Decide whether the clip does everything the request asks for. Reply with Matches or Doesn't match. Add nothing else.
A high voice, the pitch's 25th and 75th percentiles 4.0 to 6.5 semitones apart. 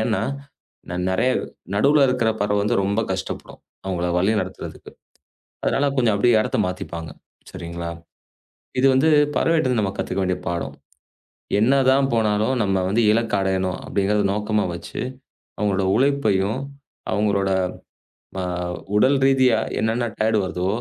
Doesn't match